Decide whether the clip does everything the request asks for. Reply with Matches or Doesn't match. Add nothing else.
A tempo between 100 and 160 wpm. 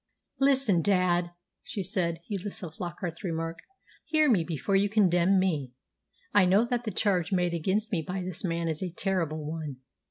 Doesn't match